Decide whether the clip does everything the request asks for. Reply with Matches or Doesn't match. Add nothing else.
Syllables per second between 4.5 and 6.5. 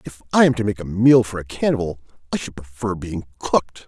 Matches